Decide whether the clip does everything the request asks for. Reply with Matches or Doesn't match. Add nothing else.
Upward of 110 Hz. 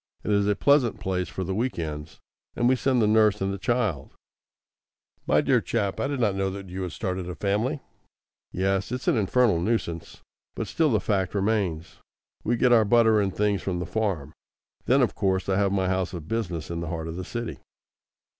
Doesn't match